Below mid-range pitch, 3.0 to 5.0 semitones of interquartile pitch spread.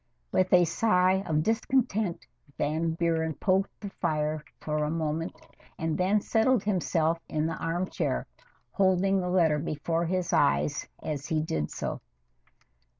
No: medium, 170 Hz; average, 3.3 semitones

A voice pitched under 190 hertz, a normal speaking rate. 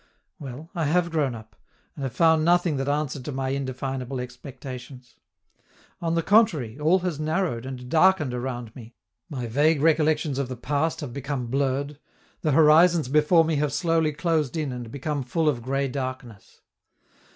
Yes: medium, 140 Hz; average, 165 wpm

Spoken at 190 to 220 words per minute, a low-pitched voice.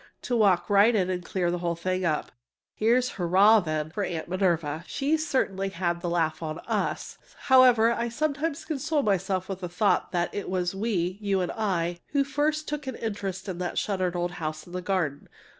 No: average, 195 wpm; high, 190 Hz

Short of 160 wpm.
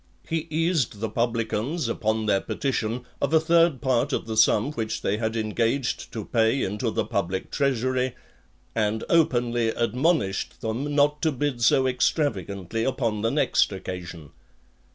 Yes: average, 150 wpm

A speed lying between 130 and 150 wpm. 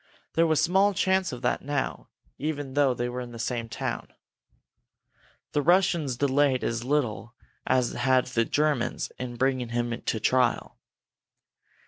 Yes: average, 145 wpm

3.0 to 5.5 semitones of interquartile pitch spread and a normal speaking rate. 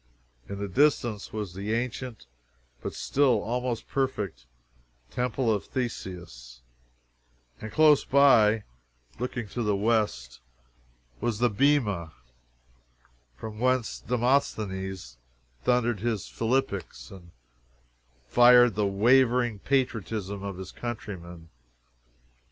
No: average, 4.1 semitones; slow, 100 wpm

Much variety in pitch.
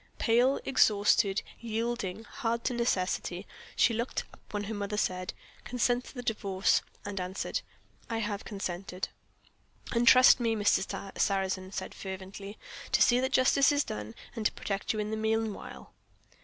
No: average, 3.3 semitones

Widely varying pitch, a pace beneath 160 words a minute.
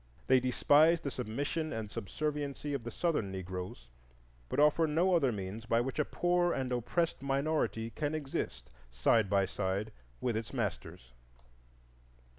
Yes: wide, 5.9 semitones; average, 145 wpm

